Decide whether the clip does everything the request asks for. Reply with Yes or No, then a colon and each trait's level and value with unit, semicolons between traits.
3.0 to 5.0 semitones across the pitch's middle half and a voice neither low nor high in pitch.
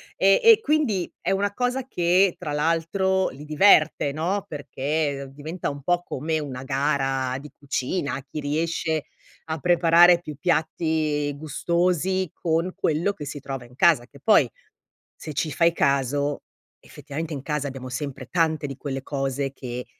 Yes: average, 3.8 semitones; medium, 155 Hz